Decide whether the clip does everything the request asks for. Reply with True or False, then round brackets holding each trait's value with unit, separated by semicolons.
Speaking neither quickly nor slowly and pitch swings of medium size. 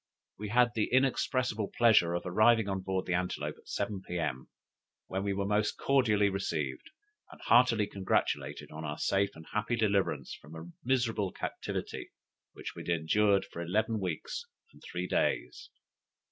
True (160 wpm; 3.9 semitones)